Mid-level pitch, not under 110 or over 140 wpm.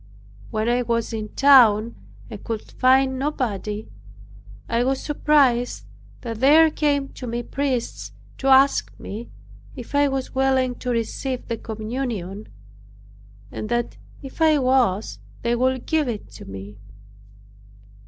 No: high, 245 Hz; slow, 135 wpm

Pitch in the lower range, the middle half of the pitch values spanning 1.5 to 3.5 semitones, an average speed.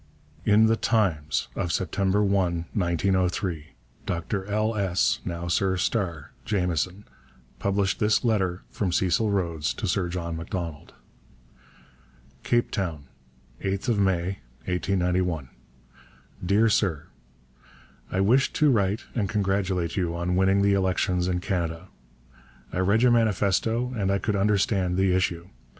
No: very low, 95 Hz; average, 2.7 semitones; slow, 125 wpm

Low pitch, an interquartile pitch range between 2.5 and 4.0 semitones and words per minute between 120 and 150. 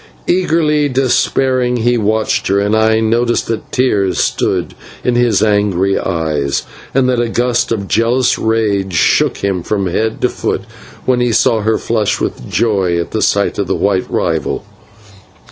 No: low, 110 Hz; average, 3.5 semitones; average, 160 wpm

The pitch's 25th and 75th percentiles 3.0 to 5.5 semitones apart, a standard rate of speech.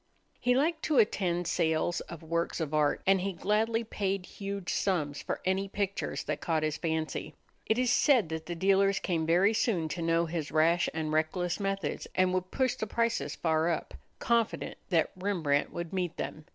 Yes: average, 3.7 semitones; average, 185 wpm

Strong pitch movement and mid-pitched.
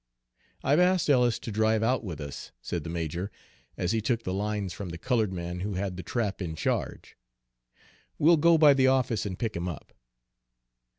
No: wide, 5.8 semitones; low, 105 Hz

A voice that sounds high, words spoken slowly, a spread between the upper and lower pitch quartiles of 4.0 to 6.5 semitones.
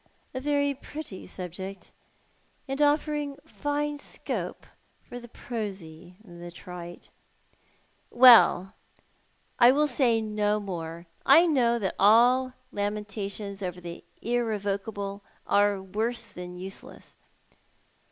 Yes: high, 210 Hz; slow, 110 wpm; average, 5.1 semitones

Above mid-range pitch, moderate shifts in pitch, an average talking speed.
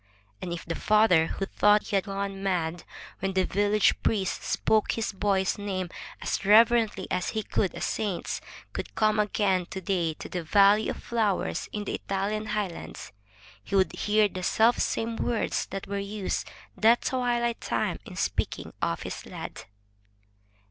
No: high, 200 Hz; narrow, 2.2 semitones; average, 160 wpm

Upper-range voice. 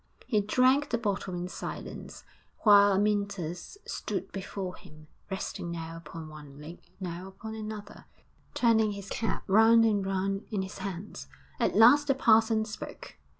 Yes: high, 200 Hz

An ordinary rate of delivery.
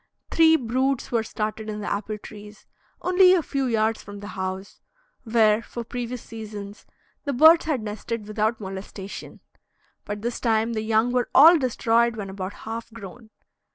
Yes: average, 160 wpm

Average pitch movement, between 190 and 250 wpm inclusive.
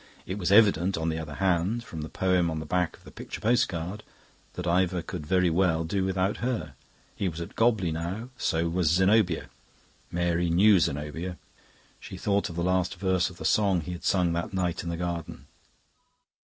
No: narrow, 2.2 semitones; average, 195 wpm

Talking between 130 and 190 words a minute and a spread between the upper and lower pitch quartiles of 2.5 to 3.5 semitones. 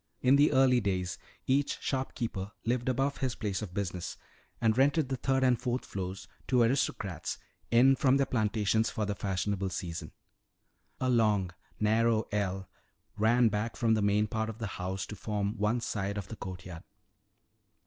No: average, 165 wpm; average, 4.0 semitones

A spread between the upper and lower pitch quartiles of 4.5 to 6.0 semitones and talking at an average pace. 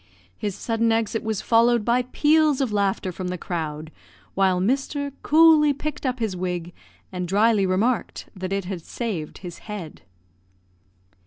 Yes: average, 5.3 semitones; average, 150 wpm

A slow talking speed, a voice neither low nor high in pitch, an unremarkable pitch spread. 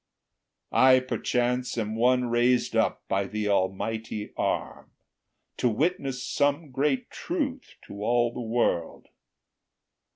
No: slow, 110 wpm; low, 125 Hz; average, 3.2 semitones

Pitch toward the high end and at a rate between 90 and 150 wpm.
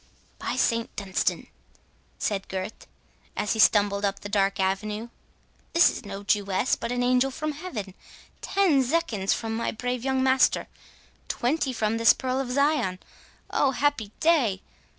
Yes: high, 230 Hz; average, 140 wpm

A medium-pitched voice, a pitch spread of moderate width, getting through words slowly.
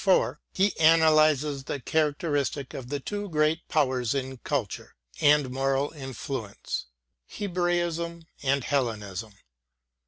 Yes: medium, 145 Hz; average, 3.4 semitones; slow, 105 wpm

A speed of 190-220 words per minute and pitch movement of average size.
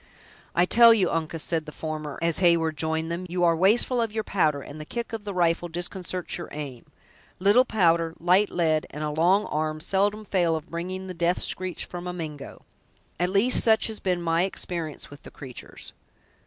Yes: average, 195 wpm; average, 3.1 semitones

